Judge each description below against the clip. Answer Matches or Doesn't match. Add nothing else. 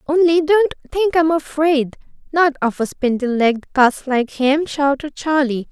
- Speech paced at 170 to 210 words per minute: Doesn't match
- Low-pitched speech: Doesn't match